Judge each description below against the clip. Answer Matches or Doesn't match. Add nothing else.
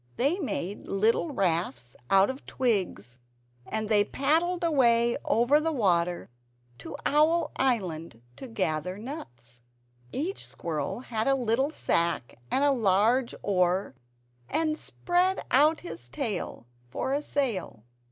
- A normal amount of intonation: Doesn't match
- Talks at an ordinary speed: Doesn't match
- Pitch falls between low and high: Doesn't match